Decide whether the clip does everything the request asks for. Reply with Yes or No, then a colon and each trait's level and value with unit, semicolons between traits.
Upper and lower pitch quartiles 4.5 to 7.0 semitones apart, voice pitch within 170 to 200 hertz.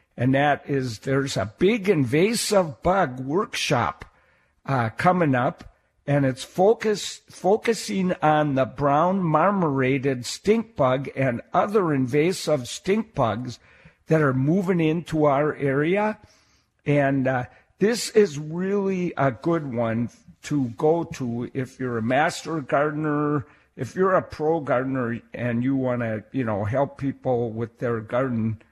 No: average, 4.9 semitones; medium, 140 Hz